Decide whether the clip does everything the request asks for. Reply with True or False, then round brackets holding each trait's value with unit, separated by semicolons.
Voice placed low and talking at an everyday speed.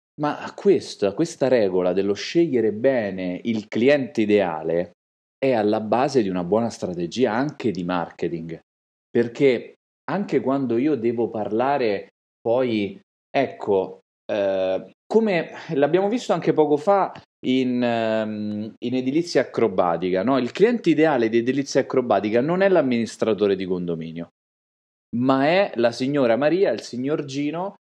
True (120 Hz; 130 wpm)